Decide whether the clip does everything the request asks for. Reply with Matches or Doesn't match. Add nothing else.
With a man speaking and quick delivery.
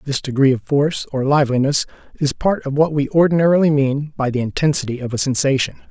Doesn't match